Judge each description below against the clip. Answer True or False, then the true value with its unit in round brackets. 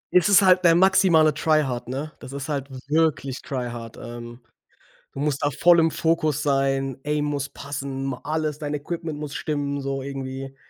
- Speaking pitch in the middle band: True (145 Hz)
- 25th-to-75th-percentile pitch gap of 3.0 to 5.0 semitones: False (2.6 semitones)